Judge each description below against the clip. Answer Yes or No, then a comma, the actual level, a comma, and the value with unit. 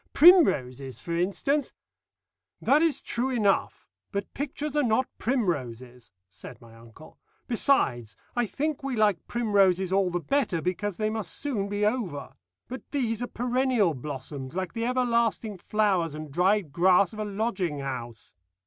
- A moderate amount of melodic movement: No, wide, 7.6 semitones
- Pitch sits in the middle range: No, high, 200 Hz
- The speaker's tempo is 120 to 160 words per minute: Yes, average, 150 wpm